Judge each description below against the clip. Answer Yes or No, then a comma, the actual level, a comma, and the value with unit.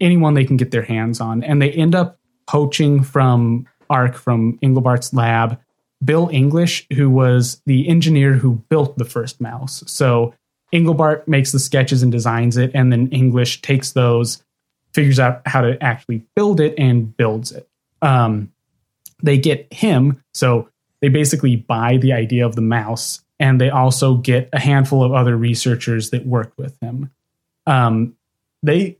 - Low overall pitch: Yes, low, 130 Hz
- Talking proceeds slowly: No, average, 165 wpm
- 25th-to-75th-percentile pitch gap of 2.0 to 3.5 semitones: Yes, average, 3.1 semitones